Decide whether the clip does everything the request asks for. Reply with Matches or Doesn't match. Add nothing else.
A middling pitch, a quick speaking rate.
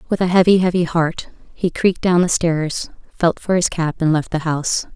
Matches